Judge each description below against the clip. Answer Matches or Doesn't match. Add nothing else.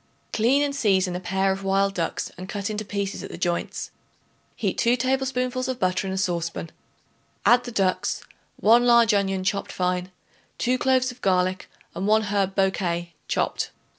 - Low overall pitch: Doesn't match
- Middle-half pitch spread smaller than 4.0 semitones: Doesn't match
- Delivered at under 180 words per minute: Matches